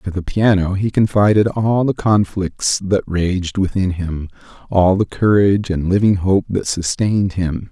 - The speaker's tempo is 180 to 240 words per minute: No, average, 165 wpm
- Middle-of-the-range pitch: No, very low, 95 Hz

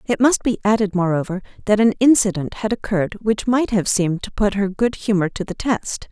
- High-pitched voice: Yes, high, 205 Hz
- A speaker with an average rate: No, fast, 215 wpm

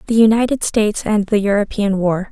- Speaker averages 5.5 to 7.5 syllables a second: Yes, 5.6 syllables/s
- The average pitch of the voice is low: No, high, 210 Hz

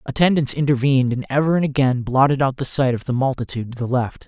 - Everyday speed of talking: No, fast, 225 wpm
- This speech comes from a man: Yes, male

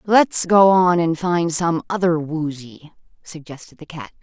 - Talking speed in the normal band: Yes, average, 155 wpm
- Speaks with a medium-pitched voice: Yes, medium, 170 Hz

